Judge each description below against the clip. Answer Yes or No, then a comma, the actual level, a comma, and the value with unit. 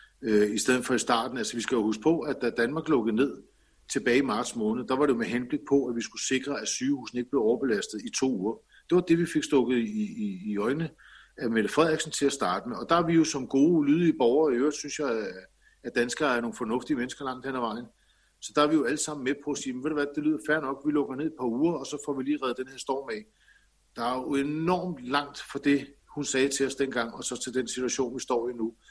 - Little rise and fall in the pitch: No, average, 3.3 semitones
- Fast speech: Yes, fast, 280 wpm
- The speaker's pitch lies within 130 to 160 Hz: Yes, medium, 140 Hz